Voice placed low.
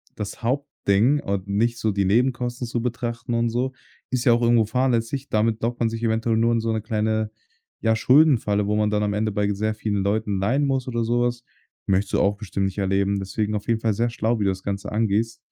Yes: low, 110 Hz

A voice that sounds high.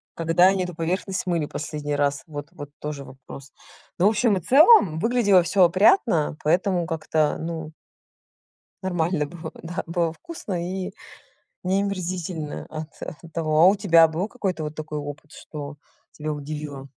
No: medium, 165 Hz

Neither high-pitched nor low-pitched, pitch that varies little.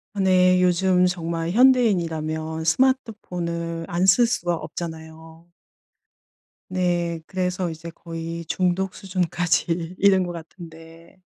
Yes: medium, 175 Hz; narrow, 2.0 semitones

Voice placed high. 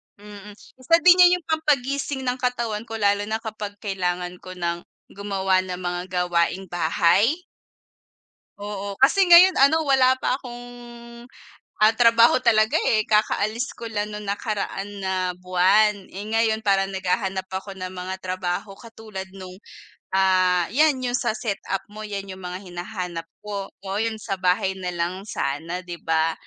Yes: high, 200 Hz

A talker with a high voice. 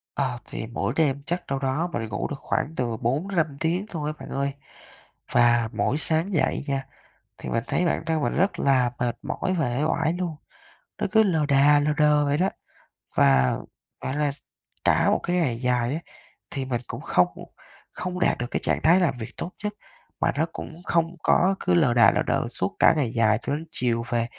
No: medium, 145 Hz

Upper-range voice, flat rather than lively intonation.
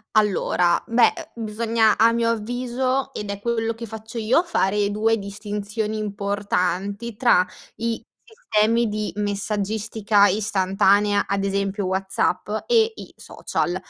Yes: high, 210 Hz; narrow, 2.3 semitones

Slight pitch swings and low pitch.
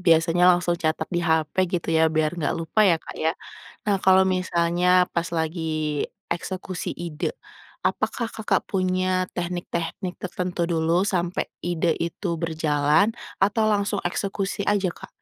No: narrow, 2.3 semitones; medium, 175 Hz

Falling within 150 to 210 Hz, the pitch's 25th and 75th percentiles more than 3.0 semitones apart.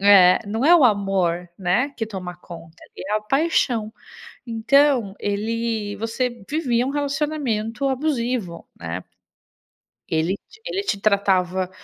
No: high, 220 Hz; wide, 5.5 semitones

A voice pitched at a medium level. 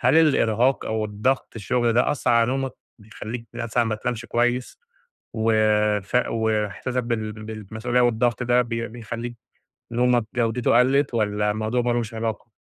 No: low, 115 Hz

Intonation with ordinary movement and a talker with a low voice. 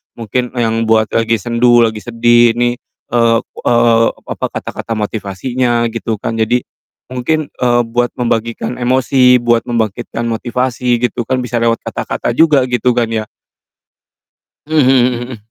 No: narrow, 1.4 semitones; low, 120 Hz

